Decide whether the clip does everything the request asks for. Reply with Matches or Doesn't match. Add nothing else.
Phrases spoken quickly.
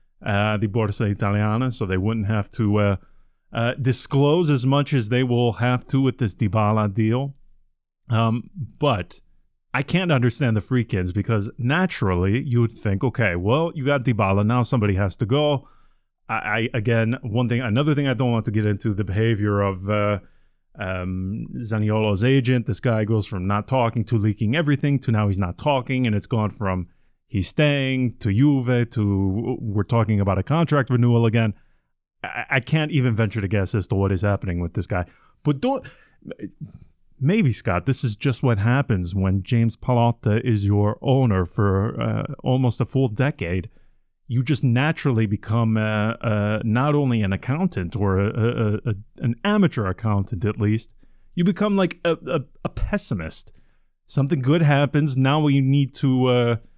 Doesn't match